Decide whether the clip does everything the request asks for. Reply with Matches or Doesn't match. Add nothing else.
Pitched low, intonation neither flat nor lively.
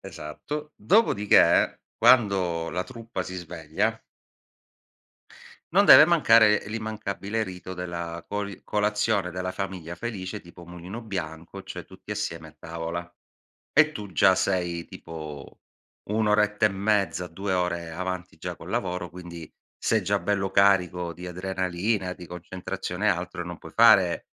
Matches